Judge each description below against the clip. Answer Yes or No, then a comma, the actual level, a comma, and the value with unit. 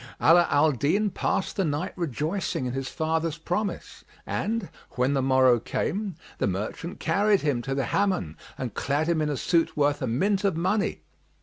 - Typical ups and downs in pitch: No, wide, 5.9 semitones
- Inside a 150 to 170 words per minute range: No, average, 180 wpm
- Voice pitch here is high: No, medium, 155 Hz